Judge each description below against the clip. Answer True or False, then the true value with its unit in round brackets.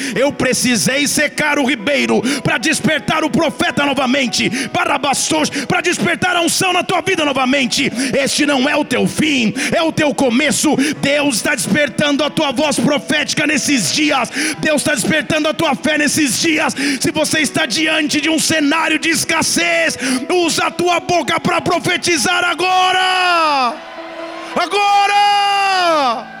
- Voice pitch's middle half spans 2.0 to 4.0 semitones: True (3.3 semitones)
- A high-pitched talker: True (300 Hz)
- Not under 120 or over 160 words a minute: True (145 wpm)